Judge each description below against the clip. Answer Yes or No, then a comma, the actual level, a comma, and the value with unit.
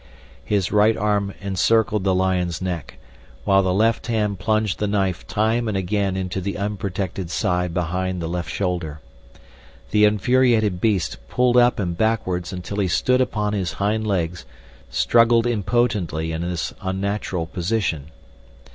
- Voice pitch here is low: Yes, low, 100 Hz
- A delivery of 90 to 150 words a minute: Yes, average, 145 wpm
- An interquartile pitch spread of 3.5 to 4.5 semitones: No, average, 3.1 semitones